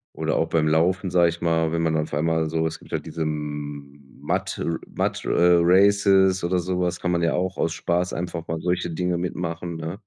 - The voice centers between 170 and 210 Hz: No, very low, 85 Hz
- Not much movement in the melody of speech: Yes, narrow, 1.9 semitones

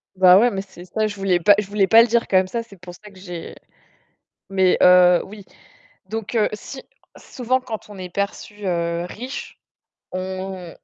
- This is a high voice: Yes, high, 195 Hz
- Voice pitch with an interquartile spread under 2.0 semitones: No, average, 2.9 semitones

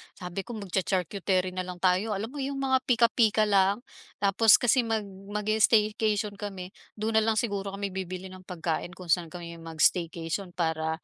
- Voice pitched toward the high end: Yes, high, 195 Hz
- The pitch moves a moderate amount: Yes, average, 3.1 semitones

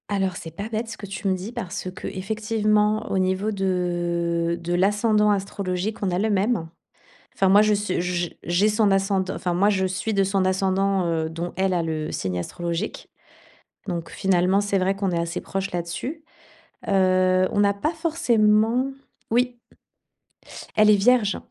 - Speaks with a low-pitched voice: No, high, 195 Hz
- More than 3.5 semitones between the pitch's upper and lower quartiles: No, average, 2.7 semitones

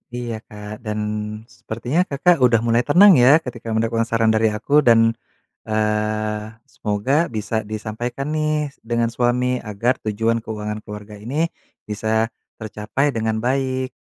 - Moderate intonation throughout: Yes, average, 3.1 semitones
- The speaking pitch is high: No, low, 115 Hz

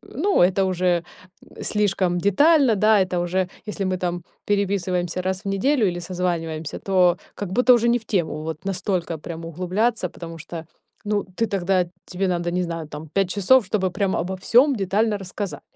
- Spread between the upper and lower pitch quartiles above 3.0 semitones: No, average, 2.7 semitones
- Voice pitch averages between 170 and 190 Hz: Yes, medium, 185 Hz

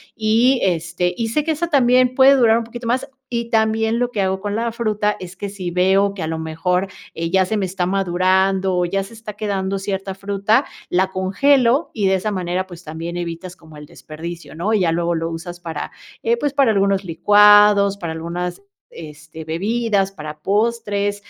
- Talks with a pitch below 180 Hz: No, high, 195 Hz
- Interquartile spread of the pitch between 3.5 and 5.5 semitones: Yes, average, 4.0 semitones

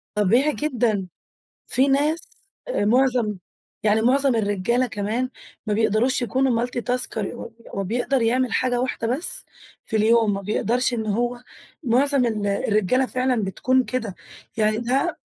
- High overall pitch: Yes, high, 240 Hz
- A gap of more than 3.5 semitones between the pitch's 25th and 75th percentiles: No, average, 3.2 semitones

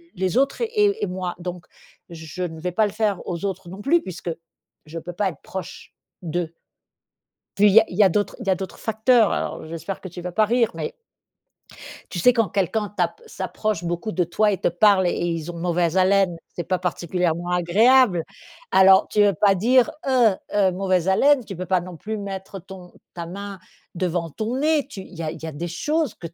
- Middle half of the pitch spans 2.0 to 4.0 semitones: Yes, average, 3.5 semitones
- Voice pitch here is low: No, high, 190 Hz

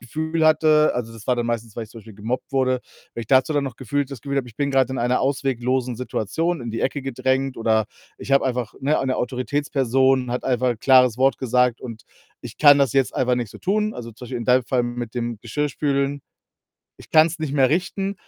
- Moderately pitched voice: No, low, 130 Hz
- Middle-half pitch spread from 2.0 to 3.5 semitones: Yes, average, 2.7 semitones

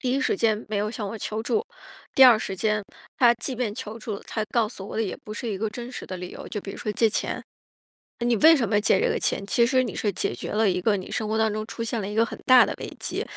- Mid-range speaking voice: No, high, 220 Hz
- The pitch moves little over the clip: Yes, narrow, 2.3 semitones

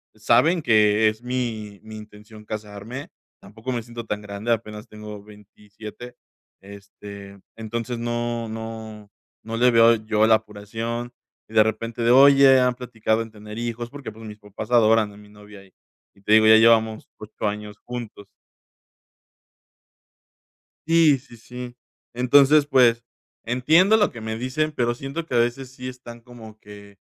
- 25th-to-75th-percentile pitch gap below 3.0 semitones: Yes, narrow, 2.5 semitones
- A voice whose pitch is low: Yes, low, 115 Hz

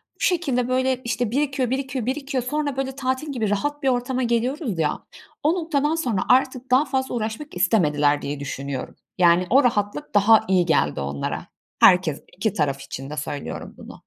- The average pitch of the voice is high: Yes, high, 245 Hz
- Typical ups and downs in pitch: No, wide, 7.0 semitones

